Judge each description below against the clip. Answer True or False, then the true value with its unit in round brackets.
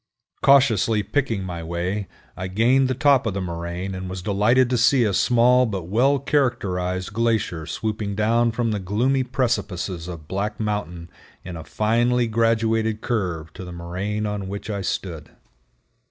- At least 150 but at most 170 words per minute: True (160 wpm)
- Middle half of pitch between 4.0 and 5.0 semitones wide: True (4.4 semitones)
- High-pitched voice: False (105 Hz)